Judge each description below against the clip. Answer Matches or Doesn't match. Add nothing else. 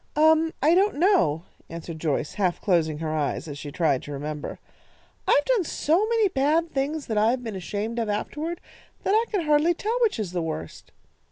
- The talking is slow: Doesn't match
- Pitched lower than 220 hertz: Doesn't match